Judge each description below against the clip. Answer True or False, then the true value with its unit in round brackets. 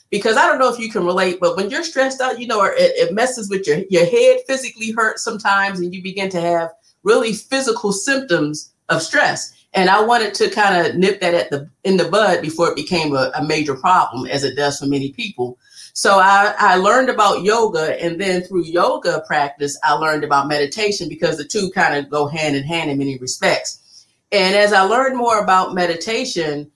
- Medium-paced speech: False (215 wpm)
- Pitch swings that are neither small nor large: False (5.9 semitones)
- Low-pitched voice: False (185 Hz)